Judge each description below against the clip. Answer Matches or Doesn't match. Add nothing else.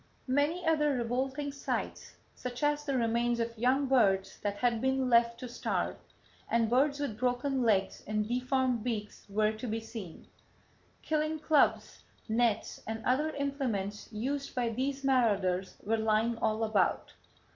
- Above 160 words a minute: Doesn't match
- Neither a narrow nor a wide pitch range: Matches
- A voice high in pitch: Matches